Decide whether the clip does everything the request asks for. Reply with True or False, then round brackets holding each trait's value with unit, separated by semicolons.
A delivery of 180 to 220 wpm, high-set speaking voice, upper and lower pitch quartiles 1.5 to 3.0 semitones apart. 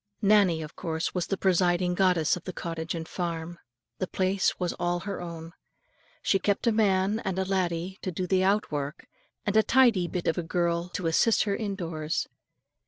False (195 wpm; 180 Hz; 2.5 semitones)